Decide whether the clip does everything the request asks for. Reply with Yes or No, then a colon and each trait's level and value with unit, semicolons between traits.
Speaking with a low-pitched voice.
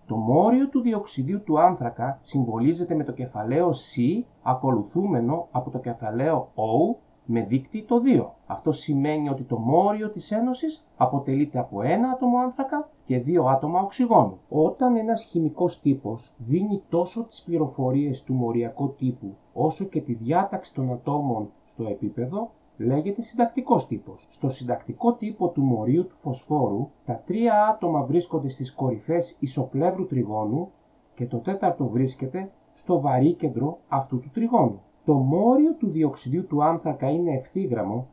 No: medium, 150 Hz